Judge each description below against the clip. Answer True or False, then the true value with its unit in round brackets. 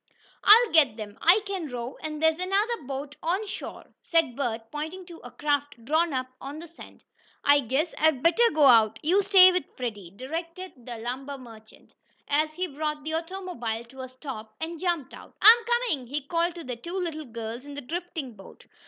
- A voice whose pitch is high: True (300 Hz)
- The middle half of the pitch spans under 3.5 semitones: False (5.5 semitones)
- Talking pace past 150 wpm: True (195 wpm)